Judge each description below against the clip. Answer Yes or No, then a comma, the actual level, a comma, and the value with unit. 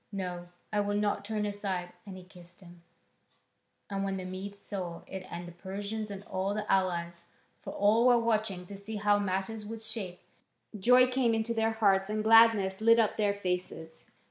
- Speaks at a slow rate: No, average, 185 wpm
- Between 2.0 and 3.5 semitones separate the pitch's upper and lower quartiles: Yes, average, 2.9 semitones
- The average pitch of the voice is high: Yes, high, 200 Hz